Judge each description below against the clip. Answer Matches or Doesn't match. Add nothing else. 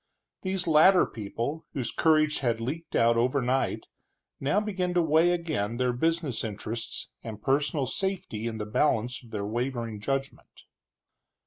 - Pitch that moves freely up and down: Matches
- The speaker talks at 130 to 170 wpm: Matches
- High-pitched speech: Doesn't match